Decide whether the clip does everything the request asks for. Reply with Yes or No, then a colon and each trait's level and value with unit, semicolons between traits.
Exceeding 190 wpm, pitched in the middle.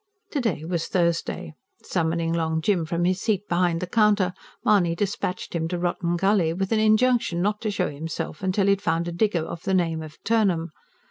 Yes: average, 200 wpm; medium, 175 Hz